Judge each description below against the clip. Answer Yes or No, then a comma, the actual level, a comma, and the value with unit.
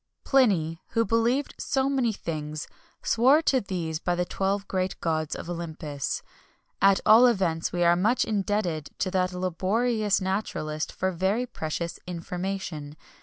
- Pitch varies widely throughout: No, average, 4.7 semitones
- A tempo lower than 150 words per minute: Yes, average, 140 wpm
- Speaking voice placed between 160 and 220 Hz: Yes, medium, 185 Hz